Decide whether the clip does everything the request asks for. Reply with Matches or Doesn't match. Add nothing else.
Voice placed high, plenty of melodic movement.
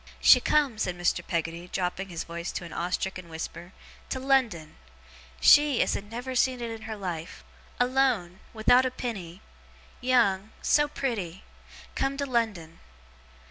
Matches